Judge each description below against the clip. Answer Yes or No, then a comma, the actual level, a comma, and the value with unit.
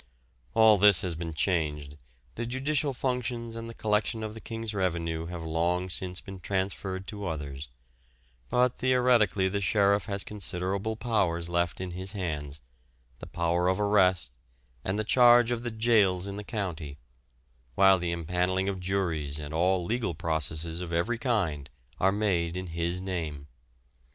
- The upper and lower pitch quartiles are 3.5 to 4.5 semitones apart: Yes, average, 4.2 semitones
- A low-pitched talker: Yes, very low, 95 Hz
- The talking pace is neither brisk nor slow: Yes, average, 155 wpm